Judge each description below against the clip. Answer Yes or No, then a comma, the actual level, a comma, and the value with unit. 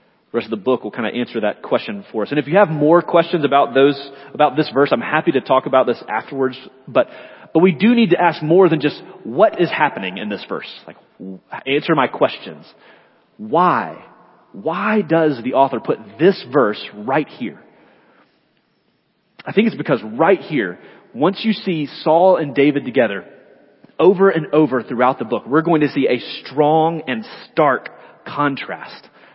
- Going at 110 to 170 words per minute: No, average, 180 wpm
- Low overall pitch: No, medium, 150 Hz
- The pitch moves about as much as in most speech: Yes, average, 4.4 semitones